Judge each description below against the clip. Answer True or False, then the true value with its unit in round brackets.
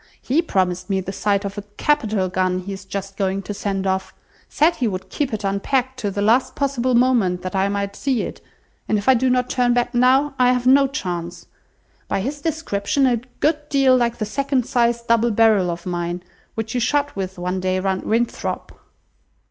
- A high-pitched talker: True (220 Hz)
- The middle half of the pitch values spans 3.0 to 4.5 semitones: False (5.1 semitones)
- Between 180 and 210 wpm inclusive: True (205 wpm)